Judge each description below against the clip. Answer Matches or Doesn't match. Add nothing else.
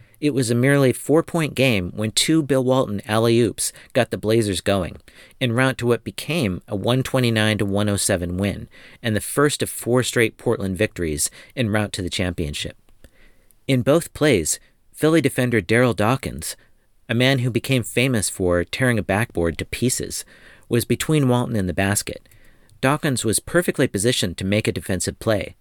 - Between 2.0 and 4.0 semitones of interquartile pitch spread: Doesn't match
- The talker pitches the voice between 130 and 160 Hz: Doesn't match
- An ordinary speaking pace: Matches